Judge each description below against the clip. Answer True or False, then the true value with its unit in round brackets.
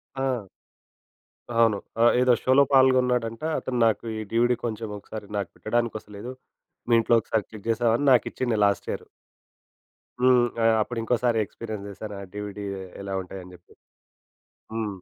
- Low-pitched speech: True (115 Hz)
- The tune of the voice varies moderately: True (3.0 semitones)